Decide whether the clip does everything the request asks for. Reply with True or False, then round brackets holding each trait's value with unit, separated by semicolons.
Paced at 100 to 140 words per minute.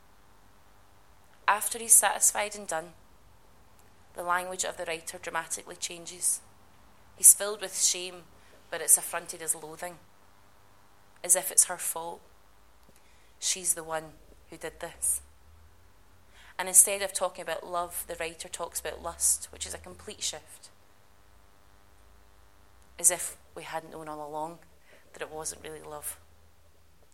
True (135 wpm)